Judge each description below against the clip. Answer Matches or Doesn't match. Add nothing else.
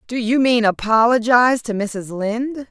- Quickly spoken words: Doesn't match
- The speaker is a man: Doesn't match